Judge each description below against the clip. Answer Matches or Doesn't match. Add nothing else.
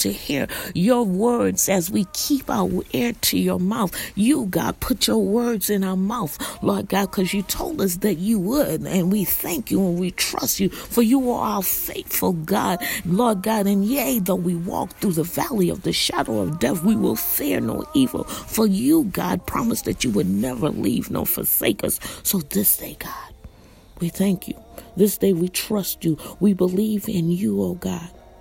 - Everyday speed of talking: Matches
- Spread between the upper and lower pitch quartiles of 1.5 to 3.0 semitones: Doesn't match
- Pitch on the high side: Matches